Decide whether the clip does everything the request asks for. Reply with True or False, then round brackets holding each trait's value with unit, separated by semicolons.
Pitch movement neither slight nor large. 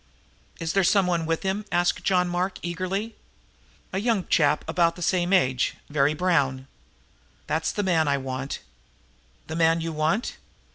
True (3.1 semitones)